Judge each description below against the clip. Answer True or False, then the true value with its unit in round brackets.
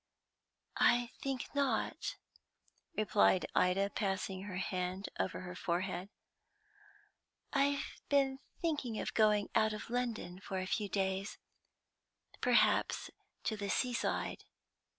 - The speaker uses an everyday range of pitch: True (4.5 semitones)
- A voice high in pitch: True (205 Hz)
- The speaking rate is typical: False (110 wpm)